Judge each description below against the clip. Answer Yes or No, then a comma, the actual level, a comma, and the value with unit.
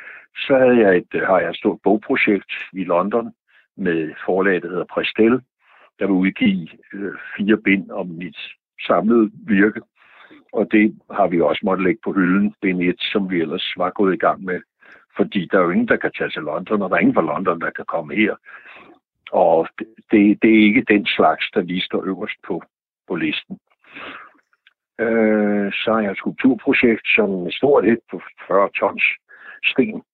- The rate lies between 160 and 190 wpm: Yes, average, 185 wpm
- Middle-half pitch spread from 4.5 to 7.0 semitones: No, average, 2.8 semitones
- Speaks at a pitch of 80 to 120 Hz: Yes, low, 105 Hz